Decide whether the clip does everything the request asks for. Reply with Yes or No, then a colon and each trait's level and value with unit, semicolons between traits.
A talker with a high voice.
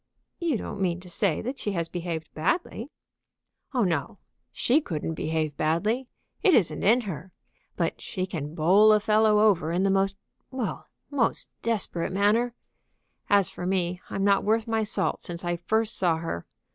Yes: high, 195 Hz